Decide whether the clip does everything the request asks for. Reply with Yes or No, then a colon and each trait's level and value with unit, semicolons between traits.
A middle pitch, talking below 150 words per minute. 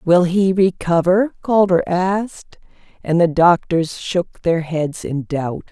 Yes: medium, 175 Hz; slow, 135 wpm